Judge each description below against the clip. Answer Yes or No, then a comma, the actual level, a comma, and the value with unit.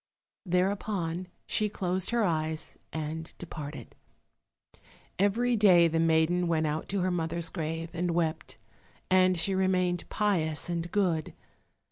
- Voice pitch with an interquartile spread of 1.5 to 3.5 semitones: Yes, narrow, 2.6 semitones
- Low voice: No, medium, 175 Hz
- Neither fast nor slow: No, slow, 125 wpm